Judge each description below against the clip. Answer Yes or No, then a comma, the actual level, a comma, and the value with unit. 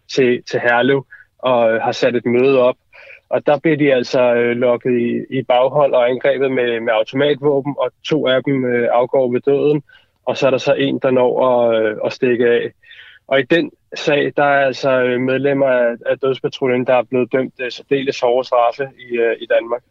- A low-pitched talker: Yes, low, 125 Hz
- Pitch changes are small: Yes, narrow, 2.2 semitones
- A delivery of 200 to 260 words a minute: No, average, 170 wpm